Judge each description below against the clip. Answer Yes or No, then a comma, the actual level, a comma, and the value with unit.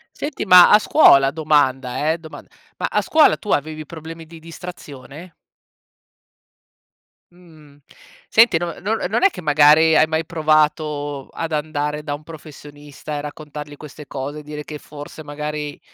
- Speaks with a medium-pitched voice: Yes, medium, 150 Hz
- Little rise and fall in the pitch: Yes, narrow, 1.9 semitones